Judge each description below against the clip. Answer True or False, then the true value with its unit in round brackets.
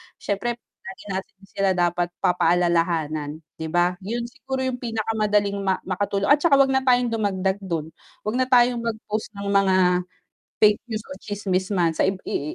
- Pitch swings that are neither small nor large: True (4.4 semitones)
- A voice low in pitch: False (200 Hz)